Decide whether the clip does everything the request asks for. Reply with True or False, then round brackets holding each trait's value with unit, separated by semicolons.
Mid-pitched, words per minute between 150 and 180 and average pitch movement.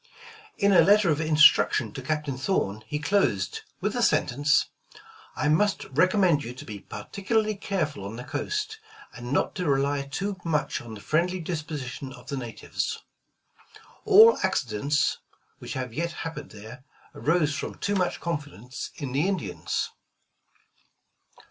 False (150 Hz; 155 wpm; 6.3 semitones)